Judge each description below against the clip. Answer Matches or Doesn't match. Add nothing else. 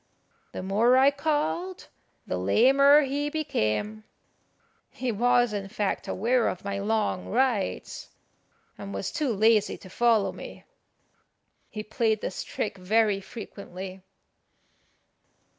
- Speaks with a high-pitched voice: Matches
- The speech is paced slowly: Matches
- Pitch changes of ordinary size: Matches